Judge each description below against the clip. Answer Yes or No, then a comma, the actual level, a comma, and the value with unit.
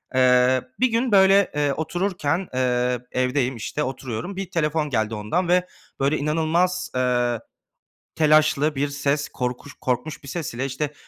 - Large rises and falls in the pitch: No, average, 4.6 semitones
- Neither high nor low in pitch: Yes, medium, 145 Hz